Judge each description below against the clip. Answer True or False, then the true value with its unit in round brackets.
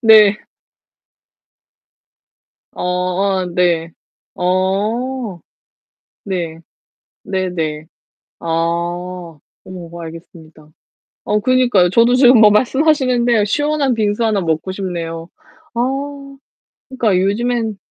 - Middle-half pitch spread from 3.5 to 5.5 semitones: True (5.1 semitones)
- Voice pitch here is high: True (195 Hz)